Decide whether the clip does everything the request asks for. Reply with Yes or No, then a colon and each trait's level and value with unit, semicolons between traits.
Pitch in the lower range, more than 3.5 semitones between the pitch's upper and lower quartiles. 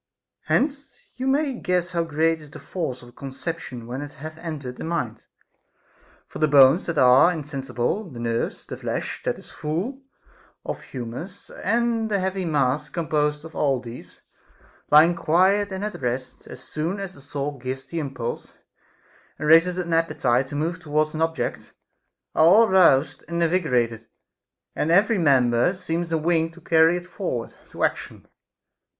No: medium, 160 Hz; average, 4.7 semitones